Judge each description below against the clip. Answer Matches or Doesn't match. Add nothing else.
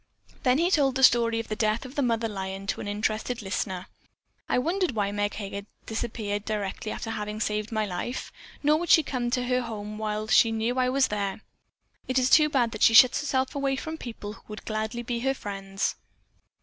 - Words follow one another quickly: Matches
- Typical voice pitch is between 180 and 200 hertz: Doesn't match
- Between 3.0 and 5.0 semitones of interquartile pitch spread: Matches